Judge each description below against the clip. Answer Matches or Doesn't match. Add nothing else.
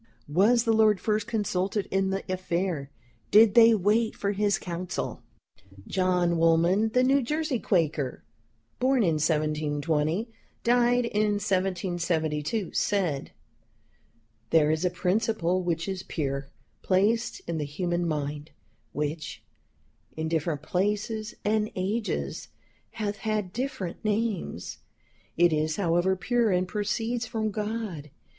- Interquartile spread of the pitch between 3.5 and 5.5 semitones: Matches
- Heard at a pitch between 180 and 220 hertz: Matches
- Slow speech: Matches